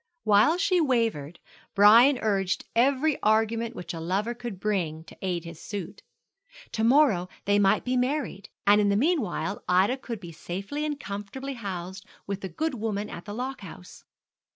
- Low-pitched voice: No, high, 210 Hz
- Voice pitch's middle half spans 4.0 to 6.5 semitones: Yes, average, 4.9 semitones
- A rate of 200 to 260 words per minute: No, average, 170 wpm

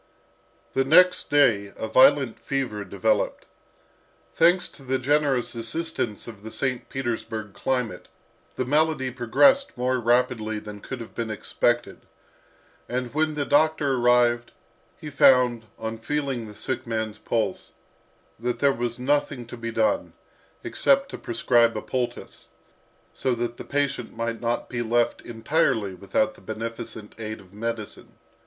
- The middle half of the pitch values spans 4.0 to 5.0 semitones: No, average, 3.5 semitones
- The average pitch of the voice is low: Yes, low, 120 Hz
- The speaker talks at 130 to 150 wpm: Yes, average, 140 wpm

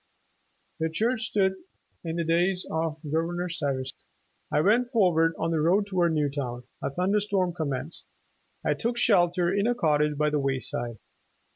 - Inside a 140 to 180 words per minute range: Yes, average, 160 wpm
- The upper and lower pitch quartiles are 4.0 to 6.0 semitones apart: Yes, average, 4.3 semitones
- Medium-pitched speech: Yes, medium, 170 Hz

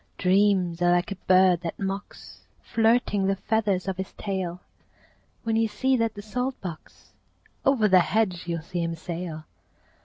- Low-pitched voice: No, high, 190 Hz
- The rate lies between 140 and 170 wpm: Yes, average, 160 wpm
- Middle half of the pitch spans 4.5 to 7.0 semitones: No, average, 3.5 semitones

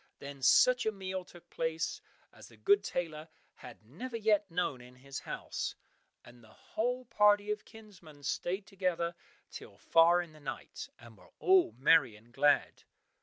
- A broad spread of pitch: Yes, wide, 7.0 semitones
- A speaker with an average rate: Yes, average, 165 wpm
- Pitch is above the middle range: No, medium, 170 Hz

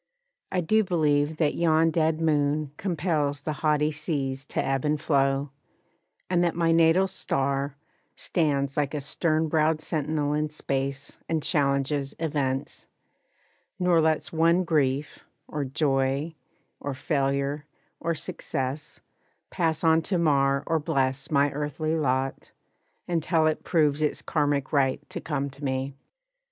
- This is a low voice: No, medium, 150 Hz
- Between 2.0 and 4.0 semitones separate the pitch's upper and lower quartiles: Yes, narrow, 2.6 semitones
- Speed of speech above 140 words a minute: No, slow, 135 wpm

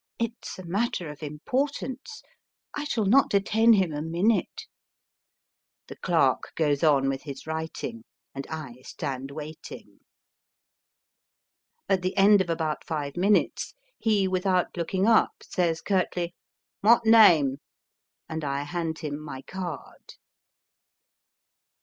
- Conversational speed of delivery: No, slow, 130 wpm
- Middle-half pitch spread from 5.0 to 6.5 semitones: Yes, average, 5.3 semitones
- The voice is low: No, medium, 175 Hz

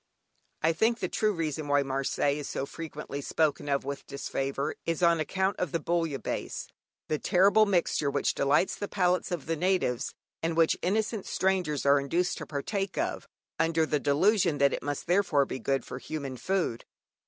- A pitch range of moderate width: Yes, average, 4.5 semitones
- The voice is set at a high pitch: No, medium, 160 Hz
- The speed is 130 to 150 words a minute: No, average, 175 wpm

